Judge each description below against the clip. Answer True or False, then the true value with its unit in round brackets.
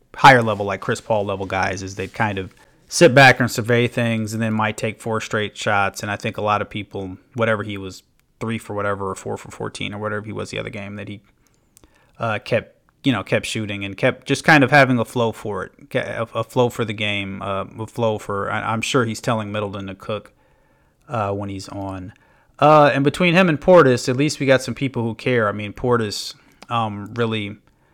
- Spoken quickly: True (230 wpm)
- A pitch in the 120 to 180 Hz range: False (110 Hz)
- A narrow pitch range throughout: False (3.2 semitones)